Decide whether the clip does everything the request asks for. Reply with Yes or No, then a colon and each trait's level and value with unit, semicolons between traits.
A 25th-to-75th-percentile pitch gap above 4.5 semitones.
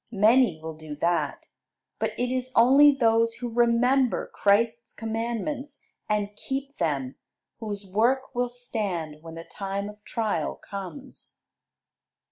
No: average, 4.0 semitones